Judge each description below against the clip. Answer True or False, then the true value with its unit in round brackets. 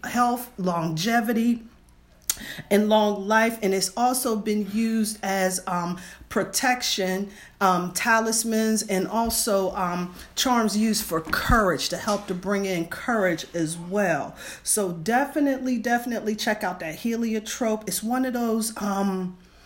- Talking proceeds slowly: True (130 wpm)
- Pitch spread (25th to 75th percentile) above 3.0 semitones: True (3.6 semitones)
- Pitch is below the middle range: False (210 Hz)